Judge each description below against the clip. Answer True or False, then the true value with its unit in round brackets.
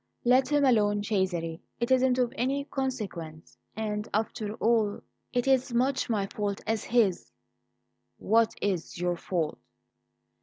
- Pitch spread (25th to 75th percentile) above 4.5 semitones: False (4.2 semitones)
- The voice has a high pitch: True (220 Hz)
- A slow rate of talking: True (130 wpm)